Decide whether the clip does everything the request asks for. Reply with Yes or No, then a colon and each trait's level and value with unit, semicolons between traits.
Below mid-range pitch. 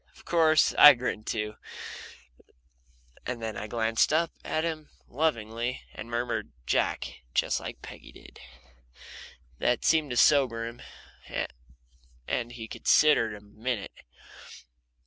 Yes: low, 120 Hz